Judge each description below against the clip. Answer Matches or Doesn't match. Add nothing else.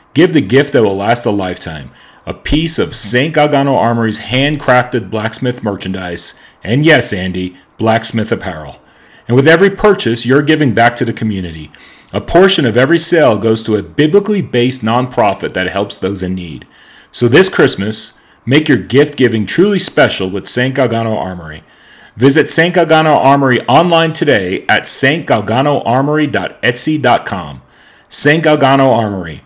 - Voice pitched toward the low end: Matches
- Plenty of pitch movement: Matches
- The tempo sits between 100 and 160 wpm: Matches